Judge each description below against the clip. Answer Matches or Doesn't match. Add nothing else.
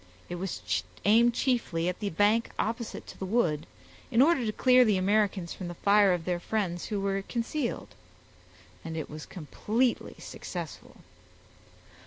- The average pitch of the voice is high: Matches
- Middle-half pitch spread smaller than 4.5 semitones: Doesn't match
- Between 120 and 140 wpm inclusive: Doesn't match